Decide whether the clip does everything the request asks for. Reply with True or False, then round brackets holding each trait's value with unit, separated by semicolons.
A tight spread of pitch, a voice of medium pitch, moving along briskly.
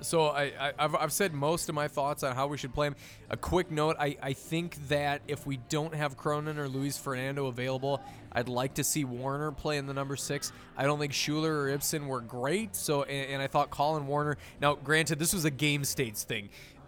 True (1.8 semitones; 145 Hz; 230 wpm)